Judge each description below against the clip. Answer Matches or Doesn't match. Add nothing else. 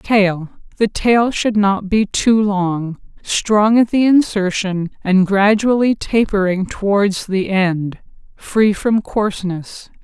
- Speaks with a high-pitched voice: Matches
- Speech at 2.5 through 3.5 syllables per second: Matches